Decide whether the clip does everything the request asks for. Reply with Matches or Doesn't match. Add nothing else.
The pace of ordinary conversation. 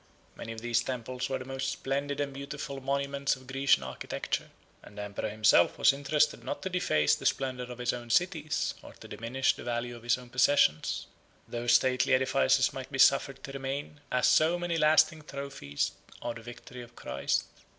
Matches